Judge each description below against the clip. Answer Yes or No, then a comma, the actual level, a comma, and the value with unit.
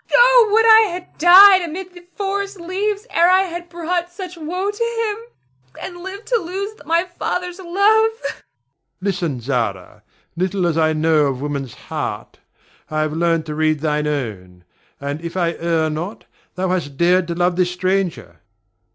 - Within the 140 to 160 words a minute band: No, average, 170 wpm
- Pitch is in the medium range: No, high, 200 Hz